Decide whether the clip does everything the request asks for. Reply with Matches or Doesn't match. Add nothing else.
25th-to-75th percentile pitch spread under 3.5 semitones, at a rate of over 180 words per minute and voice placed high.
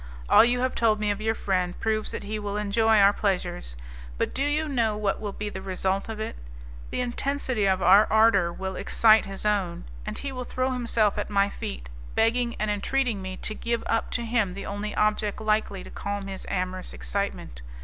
Matches